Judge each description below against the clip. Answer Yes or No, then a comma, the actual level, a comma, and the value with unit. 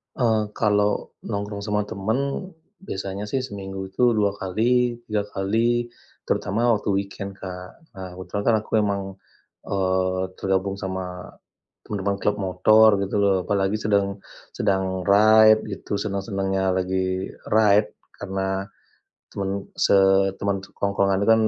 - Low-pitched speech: Yes, low, 100 Hz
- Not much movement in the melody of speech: Yes, narrow, 1.9 semitones